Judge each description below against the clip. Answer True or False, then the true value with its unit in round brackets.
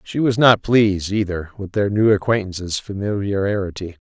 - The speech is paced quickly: False (145 wpm)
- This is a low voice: True (100 Hz)